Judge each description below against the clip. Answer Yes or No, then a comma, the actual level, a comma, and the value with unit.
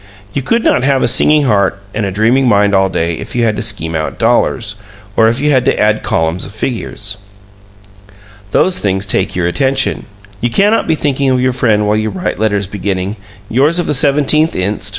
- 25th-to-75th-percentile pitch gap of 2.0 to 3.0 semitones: No, average, 5.2 semitones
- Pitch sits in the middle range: No, low, 110 Hz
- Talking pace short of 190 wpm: No, fast, 205 wpm